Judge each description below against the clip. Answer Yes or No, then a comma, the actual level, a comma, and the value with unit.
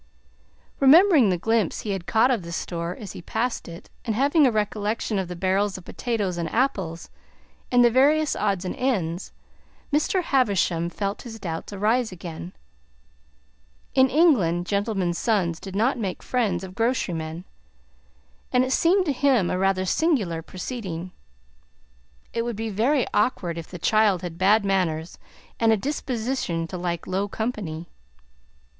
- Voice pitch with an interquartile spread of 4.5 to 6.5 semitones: Yes, wide, 5.6 semitones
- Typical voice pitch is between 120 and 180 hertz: No, high, 205 Hz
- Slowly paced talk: No, average, 155 wpm